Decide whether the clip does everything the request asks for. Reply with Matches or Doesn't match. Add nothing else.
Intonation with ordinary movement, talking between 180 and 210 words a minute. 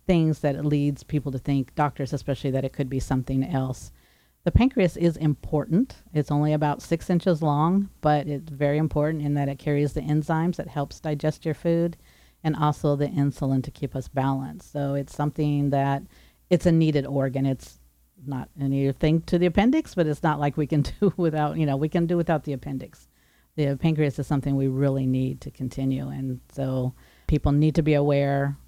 Doesn't match